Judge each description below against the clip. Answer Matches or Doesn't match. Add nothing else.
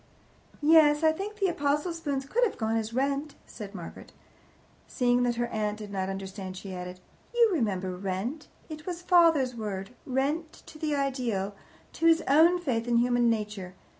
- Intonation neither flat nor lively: Doesn't match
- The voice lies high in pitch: Matches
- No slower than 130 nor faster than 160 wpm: Doesn't match